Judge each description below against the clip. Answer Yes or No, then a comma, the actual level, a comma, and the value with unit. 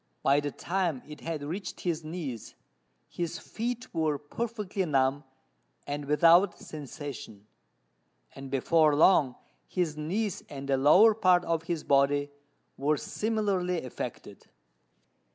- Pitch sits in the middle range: Yes, medium, 155 Hz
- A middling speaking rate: No, slow, 120 wpm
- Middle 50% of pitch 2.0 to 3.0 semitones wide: No, average, 4.2 semitones